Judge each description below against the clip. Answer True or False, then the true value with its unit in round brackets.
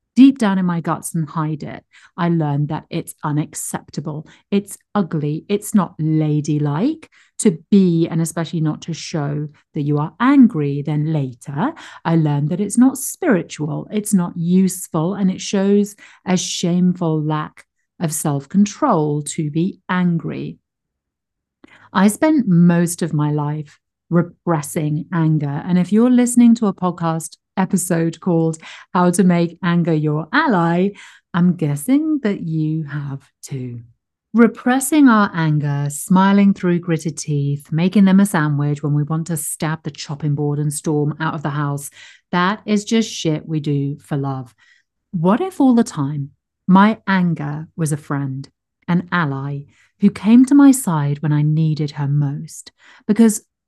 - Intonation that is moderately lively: True (4.6 semitones)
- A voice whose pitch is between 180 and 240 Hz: False (165 Hz)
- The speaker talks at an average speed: True (155 wpm)